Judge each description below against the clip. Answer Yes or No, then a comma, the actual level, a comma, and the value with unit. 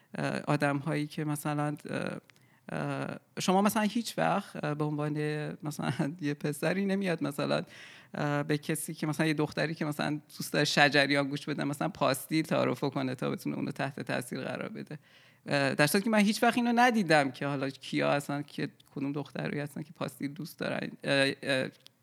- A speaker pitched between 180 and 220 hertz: No, medium, 150 Hz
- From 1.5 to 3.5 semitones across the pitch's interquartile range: Yes, narrow, 2.4 semitones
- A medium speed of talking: No, fast, 160 wpm